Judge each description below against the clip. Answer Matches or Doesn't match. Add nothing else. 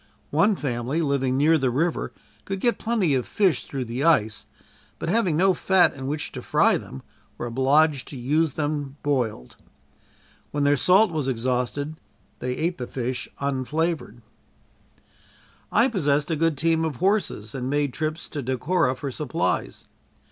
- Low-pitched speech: Doesn't match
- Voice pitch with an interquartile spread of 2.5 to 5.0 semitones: Matches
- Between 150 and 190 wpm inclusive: Matches